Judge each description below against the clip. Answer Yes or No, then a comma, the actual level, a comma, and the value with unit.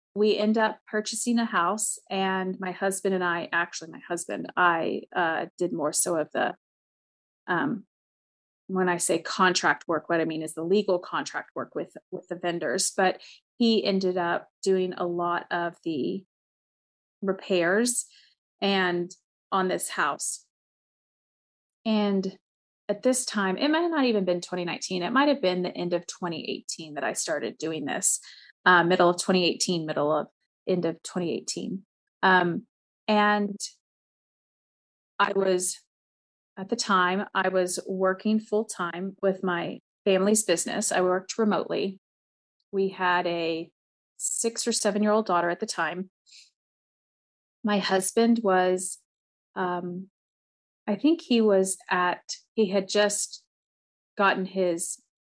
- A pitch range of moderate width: Yes, average, 3.0 semitones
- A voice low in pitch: No, high, 190 Hz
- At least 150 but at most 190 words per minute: No, average, 140 wpm